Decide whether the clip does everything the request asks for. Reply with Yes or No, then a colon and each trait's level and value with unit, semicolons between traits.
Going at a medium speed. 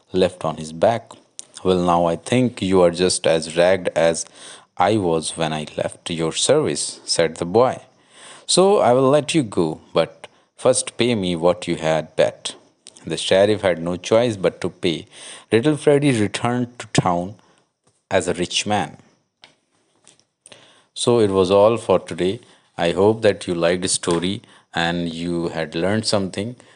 Yes: average, 165 wpm